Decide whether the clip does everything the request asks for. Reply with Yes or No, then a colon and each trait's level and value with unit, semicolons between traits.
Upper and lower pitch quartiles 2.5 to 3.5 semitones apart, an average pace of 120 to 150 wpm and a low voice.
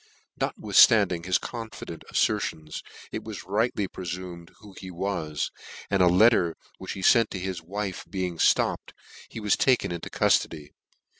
Yes: average, 3.2 semitones; average, 145 wpm; very low, 95 Hz